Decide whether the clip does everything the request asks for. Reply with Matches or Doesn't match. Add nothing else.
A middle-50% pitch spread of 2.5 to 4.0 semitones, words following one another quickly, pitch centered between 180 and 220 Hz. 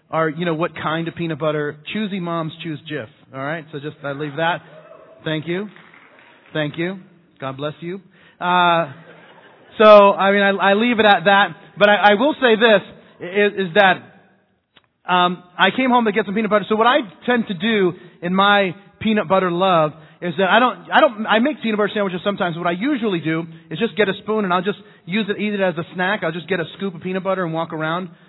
Matches